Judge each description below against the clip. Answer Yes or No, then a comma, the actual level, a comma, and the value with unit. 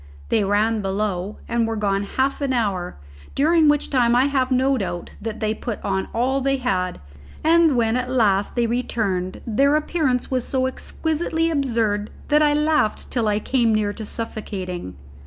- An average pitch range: Yes, average, 4.8 semitones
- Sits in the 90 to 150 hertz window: No, high, 235 Hz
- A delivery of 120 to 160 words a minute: No, average, 170 wpm